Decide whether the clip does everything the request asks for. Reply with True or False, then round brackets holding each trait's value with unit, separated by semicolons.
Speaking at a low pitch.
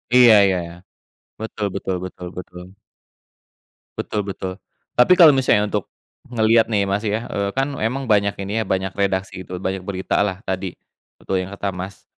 True (100 Hz)